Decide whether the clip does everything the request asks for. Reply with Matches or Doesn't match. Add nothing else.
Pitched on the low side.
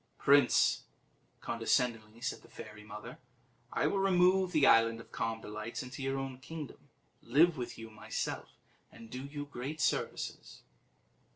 Matches